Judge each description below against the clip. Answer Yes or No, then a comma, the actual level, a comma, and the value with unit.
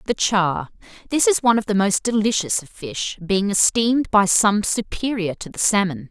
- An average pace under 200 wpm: Yes, average, 175 wpm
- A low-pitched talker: No, high, 205 Hz